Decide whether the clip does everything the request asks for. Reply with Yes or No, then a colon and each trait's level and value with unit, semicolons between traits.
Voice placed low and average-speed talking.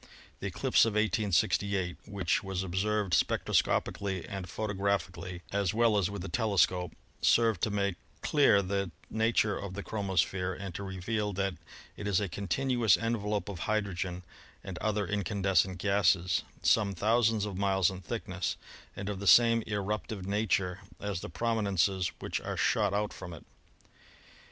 Yes: low, 100 Hz; average, 150 wpm